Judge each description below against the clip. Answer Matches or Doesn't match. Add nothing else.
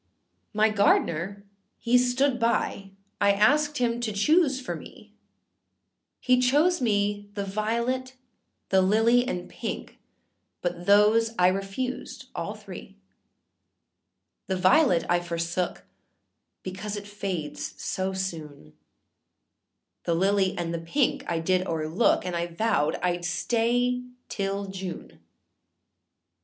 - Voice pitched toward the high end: Matches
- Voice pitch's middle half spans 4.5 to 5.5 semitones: Matches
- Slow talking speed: Matches